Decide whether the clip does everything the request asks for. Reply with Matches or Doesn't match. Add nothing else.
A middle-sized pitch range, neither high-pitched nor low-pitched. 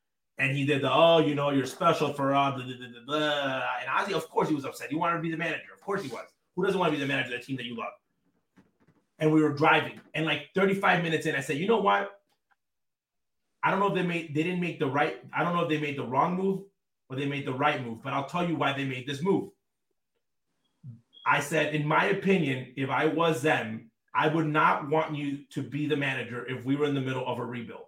Matches